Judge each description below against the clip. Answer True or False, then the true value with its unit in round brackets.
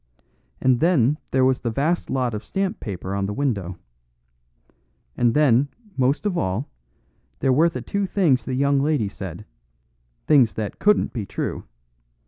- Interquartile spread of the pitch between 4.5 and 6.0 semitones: True (5.6 semitones)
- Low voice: True (130 Hz)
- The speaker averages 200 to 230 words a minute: False (155 wpm)